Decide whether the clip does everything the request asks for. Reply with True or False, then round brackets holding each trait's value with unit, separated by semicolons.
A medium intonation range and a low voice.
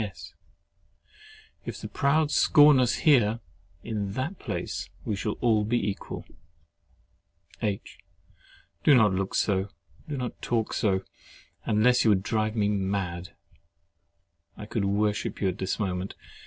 True (3.6 semitones; 105 Hz)